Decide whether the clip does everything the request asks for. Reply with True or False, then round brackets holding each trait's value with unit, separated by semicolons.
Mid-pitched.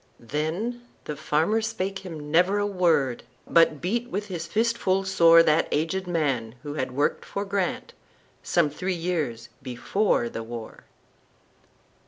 True (170 Hz)